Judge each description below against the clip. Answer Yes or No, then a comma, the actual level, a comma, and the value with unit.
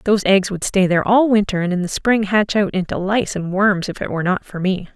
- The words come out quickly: Yes, fast, 280 wpm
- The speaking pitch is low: No, high, 195 Hz